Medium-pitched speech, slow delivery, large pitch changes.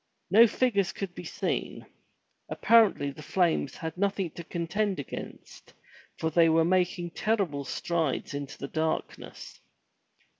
No: medium, 175 Hz; slow, 125 wpm; average, 3.8 semitones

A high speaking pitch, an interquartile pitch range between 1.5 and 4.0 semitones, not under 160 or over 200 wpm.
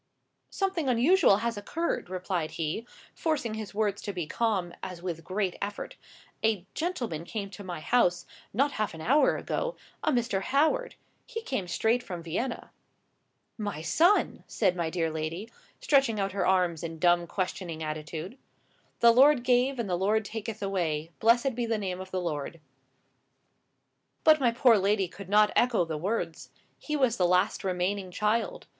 No: high, 205 Hz; average, 5.3 semitones; average, 165 wpm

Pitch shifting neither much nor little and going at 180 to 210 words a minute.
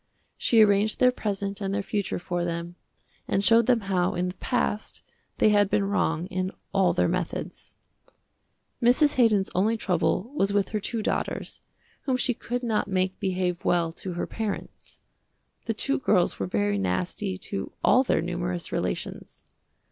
No: average, 3.6 semitones; average, 165 wpm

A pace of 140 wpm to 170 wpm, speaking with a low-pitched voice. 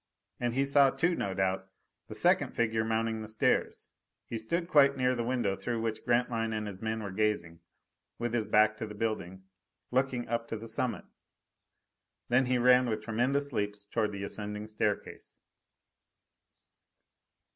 Yes: average, 160 wpm; low, 115 Hz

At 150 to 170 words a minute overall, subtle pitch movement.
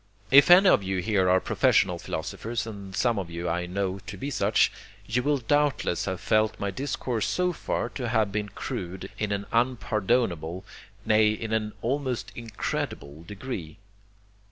No: average, 160 wpm; average, 4.5 semitones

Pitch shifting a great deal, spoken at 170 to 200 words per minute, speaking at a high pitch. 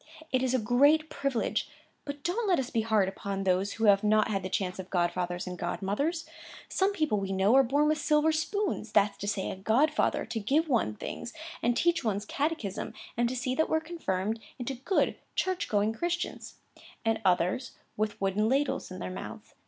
Yes: wide, 7.2 semitones; average, 185 wpm; high, 225 Hz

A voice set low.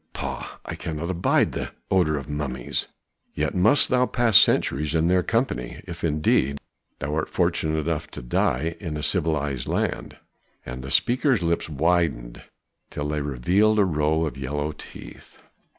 Yes: very low, 80 Hz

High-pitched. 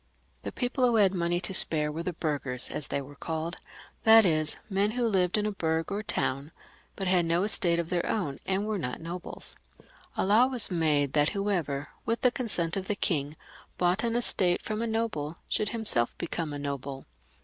No: medium, 175 Hz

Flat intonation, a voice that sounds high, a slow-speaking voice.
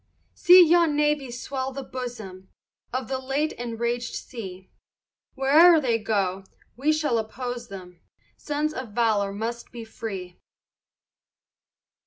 No: average, 4.3 semitones; high, 245 Hz; slow, 120 wpm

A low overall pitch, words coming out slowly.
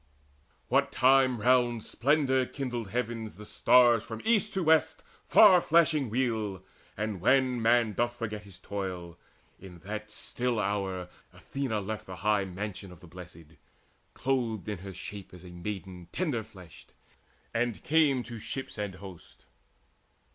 No: low, 110 Hz; average, 145 wpm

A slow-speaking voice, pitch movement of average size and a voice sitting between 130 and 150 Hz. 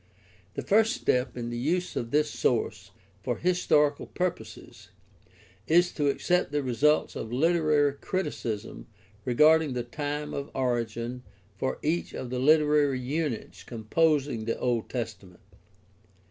Yes: slow, 130 wpm; average, 4.4 semitones; medium, 140 Hz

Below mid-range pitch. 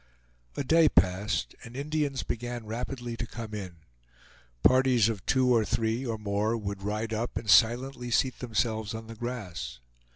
Yes: low, 115 Hz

